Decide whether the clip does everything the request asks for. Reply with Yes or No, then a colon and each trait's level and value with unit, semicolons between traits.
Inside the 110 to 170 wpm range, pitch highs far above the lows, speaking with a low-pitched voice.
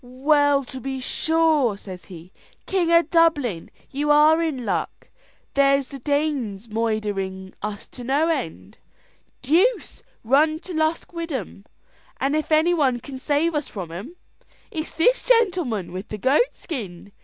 No: average, 155 wpm; wide, 6.6 semitones; very high, 275 Hz